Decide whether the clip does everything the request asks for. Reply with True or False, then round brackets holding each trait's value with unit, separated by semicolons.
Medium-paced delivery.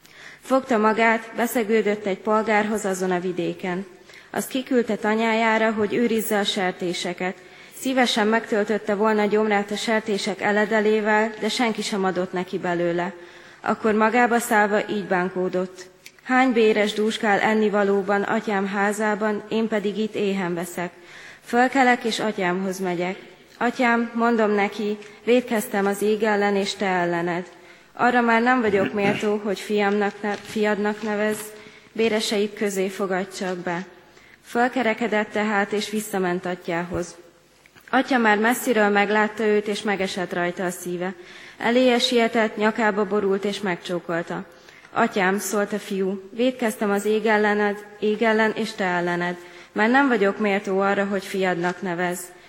True (135 wpm)